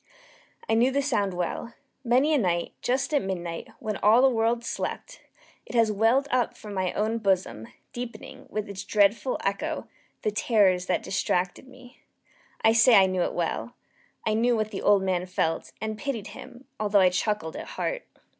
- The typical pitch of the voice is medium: No, high, 215 Hz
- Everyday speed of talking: Yes, average, 180 wpm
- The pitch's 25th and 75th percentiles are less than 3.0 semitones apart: No, average, 4.3 semitones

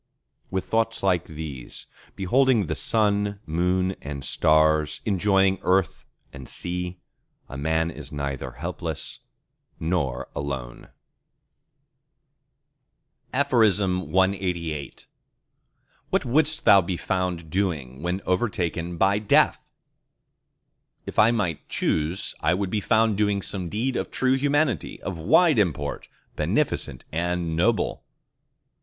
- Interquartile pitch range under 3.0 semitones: No, average, 4.3 semitones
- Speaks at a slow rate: Yes, slow, 110 wpm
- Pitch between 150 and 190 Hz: No, very low, 90 Hz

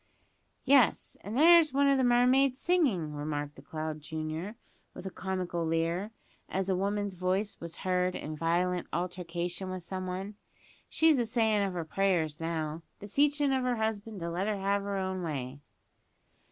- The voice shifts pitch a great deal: No, average, 4.7 semitones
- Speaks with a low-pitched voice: No, medium, 185 Hz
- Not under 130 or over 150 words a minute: No, average, 165 wpm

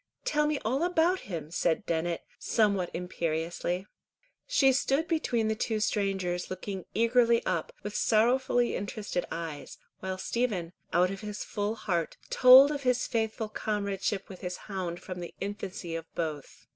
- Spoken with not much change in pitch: No, average, 4.9 semitones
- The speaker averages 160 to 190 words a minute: No, average, 150 wpm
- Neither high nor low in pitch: No, high, 205 Hz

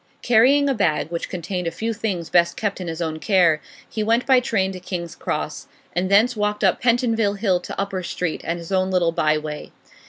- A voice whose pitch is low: No, high, 190 Hz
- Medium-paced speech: No, fast, 215 wpm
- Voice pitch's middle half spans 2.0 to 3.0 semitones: No, average, 4.4 semitones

